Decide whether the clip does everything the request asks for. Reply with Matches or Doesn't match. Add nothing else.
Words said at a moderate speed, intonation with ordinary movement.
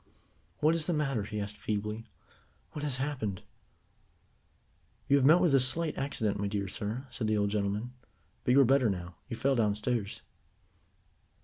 Matches